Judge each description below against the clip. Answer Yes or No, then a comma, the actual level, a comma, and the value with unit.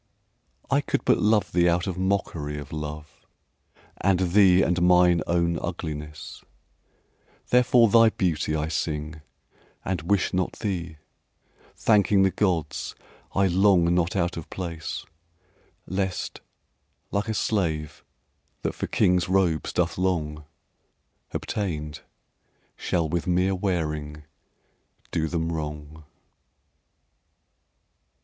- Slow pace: Yes, slow, 110 wpm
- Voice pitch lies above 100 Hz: No, very low, 85 Hz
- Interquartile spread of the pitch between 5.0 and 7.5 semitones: No, average, 3.4 semitones